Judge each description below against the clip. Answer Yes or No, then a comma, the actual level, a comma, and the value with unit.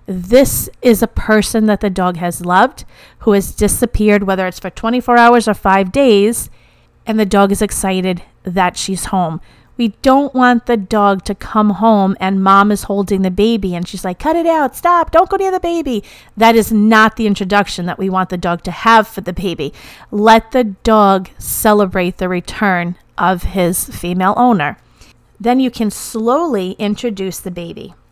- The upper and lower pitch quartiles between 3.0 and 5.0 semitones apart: Yes, average, 3.3 semitones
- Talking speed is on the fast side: No, average, 185 wpm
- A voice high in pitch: Yes, high, 205 Hz